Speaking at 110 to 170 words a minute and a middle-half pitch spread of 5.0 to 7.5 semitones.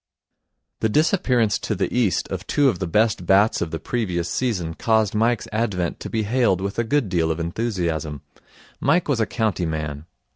No: average, 185 wpm; average, 5.3 semitones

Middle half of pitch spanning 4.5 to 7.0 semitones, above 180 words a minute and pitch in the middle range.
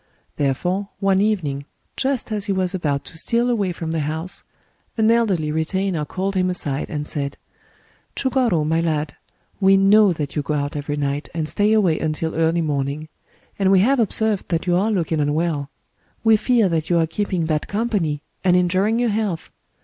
Yes: average, 4.9 semitones; average, 190 wpm; medium, 175 Hz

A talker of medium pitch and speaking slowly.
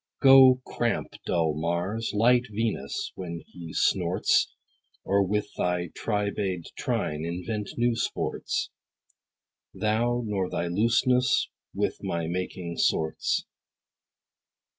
No: low, 100 Hz; slow, 100 wpm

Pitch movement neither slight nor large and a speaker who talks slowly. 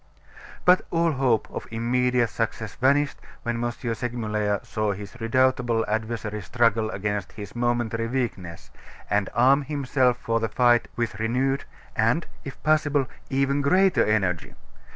Yes: average, 3.4 semitones; slow, 130 wpm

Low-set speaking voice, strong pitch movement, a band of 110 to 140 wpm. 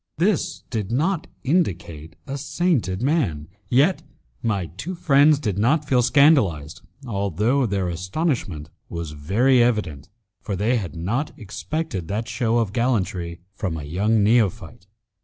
Yes: low, 110 Hz; wide, 7.6 semitones; slow, 135 wpm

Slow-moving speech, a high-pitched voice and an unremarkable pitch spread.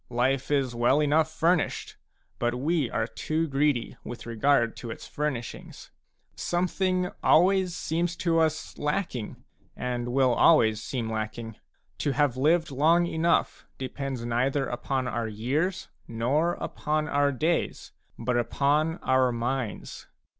No: slow, 130 wpm; medium, 140 Hz; average, 4.8 semitones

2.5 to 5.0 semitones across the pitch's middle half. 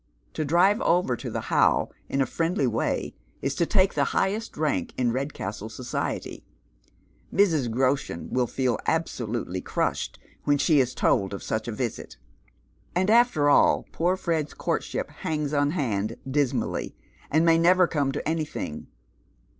No: wide, 5.5 semitones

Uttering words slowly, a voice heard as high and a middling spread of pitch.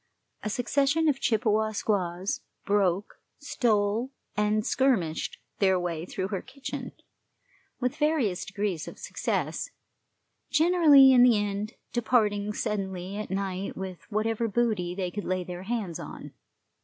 Yes: slow, 130 wpm; high, 210 Hz; average, 4.2 semitones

